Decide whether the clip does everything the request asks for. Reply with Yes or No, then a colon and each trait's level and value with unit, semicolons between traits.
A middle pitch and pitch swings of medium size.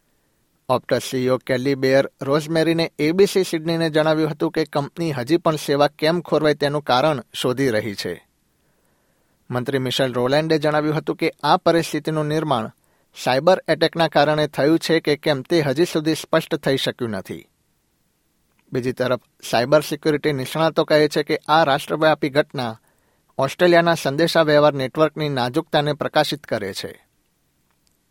Yes: medium, 150 Hz; average, 3.0 semitones